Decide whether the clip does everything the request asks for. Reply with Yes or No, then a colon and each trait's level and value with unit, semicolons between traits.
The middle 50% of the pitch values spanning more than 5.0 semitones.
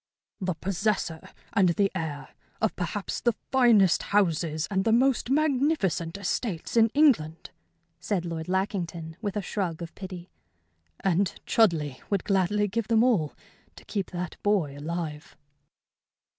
No: average, 4.3 semitones